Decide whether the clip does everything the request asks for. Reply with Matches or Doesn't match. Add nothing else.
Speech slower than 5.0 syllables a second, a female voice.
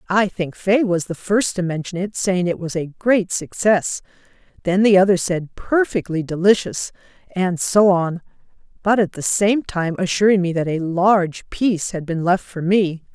Matches